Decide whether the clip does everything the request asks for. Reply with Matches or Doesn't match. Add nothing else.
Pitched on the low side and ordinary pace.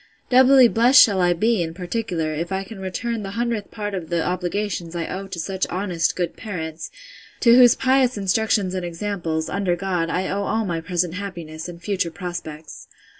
Doesn't match